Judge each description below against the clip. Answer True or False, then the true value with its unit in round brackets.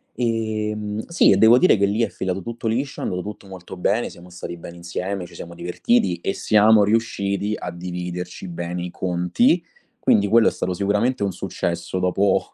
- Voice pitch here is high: False (100 Hz)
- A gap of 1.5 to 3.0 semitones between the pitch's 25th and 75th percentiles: False (3.5 semitones)